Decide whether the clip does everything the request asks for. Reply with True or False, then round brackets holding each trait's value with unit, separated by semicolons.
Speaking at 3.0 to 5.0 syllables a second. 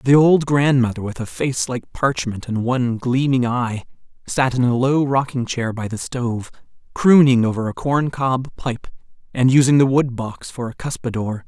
True (4.7 syllables/s)